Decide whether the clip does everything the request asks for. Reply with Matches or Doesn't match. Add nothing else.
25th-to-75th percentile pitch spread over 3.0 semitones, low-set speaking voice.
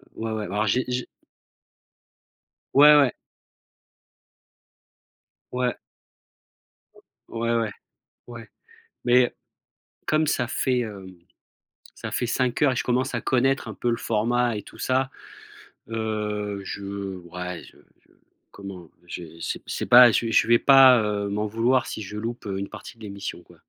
Matches